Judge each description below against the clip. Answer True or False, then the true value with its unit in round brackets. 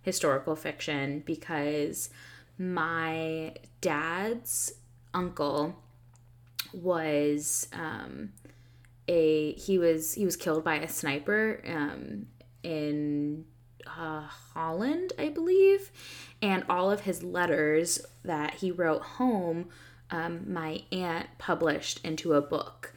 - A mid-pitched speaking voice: True (160 Hz)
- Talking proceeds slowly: True (100 wpm)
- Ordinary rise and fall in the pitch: True (3.4 semitones)